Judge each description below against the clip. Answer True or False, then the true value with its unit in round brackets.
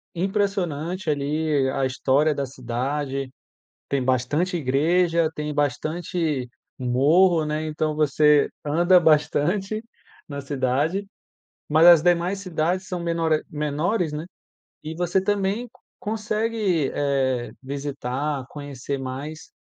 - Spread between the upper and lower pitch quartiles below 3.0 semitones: False (4.0 semitones)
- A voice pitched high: False (155 Hz)